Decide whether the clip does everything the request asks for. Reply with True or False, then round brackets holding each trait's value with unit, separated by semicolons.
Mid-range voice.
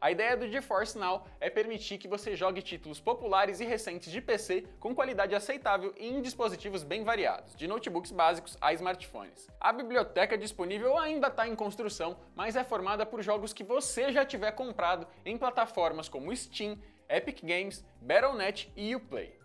False (210 Hz)